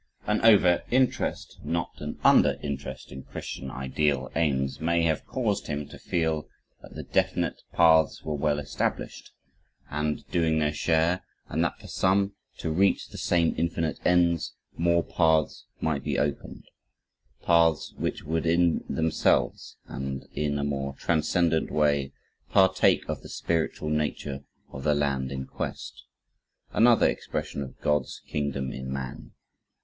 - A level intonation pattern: No, average, 3.1 semitones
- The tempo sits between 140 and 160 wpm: Yes, average, 145 wpm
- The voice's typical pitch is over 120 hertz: No, very low, 75 Hz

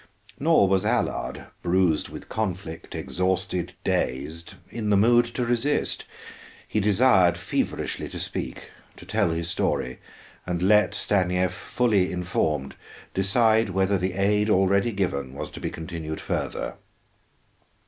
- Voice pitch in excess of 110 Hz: No, very low, 95 Hz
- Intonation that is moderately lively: Yes, average, 3.4 semitones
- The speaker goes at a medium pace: No, slow, 130 wpm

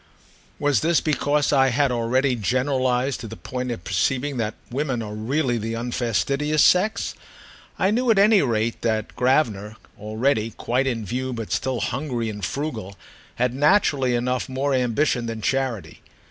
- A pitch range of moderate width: Yes, average, 3.6 semitones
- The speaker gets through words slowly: No, average, 155 wpm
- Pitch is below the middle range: Yes, low, 125 Hz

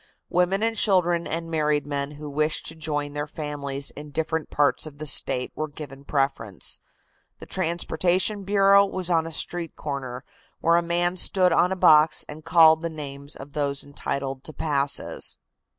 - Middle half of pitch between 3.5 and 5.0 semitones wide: No, average, 3.1 semitones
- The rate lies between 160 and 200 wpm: Yes, average, 170 wpm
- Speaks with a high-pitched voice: No, medium, 155 Hz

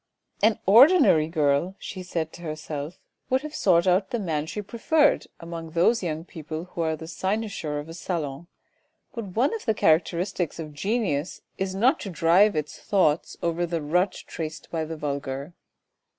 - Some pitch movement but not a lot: Yes, average, 4.2 semitones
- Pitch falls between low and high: Yes, medium, 170 Hz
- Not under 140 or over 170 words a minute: No, average, 180 wpm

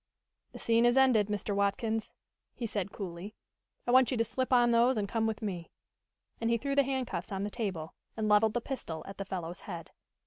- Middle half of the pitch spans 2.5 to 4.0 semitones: Yes, average, 3.4 semitones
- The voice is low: No, high, 220 Hz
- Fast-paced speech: Yes, fast, 210 wpm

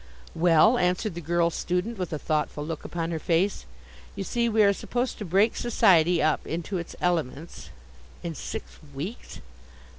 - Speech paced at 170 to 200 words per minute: No, average, 160 wpm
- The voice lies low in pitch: No, medium, 175 Hz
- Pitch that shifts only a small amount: No, average, 3.6 semitones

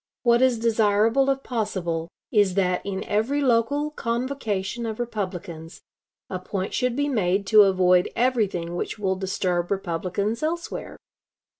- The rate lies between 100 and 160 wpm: Yes, slow, 135 wpm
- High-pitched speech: Yes, high, 210 Hz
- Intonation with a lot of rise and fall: No, average, 4.4 semitones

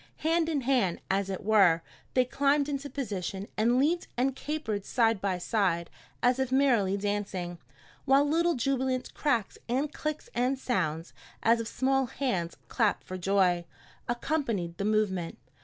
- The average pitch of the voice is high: Yes, high, 235 Hz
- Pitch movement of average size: No, wide, 5.8 semitones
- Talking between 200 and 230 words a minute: No, average, 150 wpm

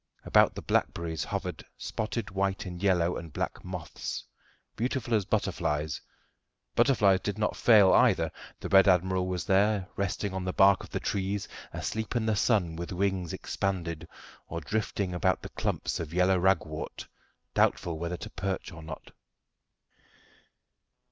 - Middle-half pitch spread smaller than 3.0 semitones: Yes, narrow, 2.6 semitones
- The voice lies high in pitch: No, very low, 95 Hz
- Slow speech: No, average, 150 wpm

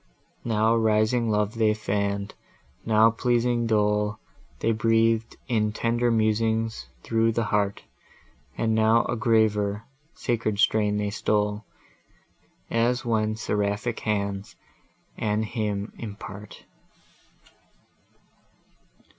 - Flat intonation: Yes, narrow, 1.5 semitones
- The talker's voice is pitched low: Yes, low, 110 Hz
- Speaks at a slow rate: Yes, slow, 95 wpm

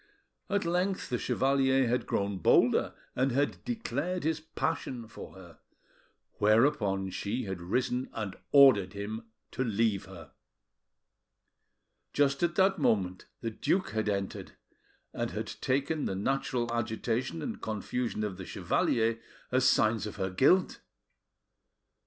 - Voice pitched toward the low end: Yes, low, 120 Hz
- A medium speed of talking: No, slow, 130 wpm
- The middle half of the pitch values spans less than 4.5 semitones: No, average, 5.3 semitones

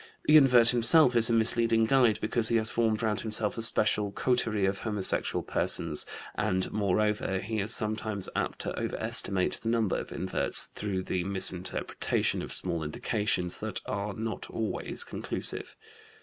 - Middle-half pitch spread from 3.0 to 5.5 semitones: No, narrow, 2.5 semitones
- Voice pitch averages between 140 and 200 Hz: No, low, 110 Hz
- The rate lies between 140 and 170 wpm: Yes, average, 155 wpm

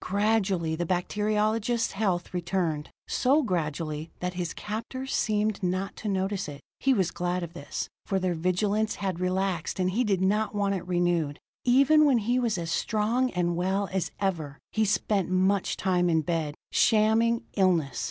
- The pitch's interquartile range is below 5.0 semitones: Yes, average, 3.6 semitones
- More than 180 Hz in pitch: Yes, high, 190 Hz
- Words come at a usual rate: Yes, average, 165 wpm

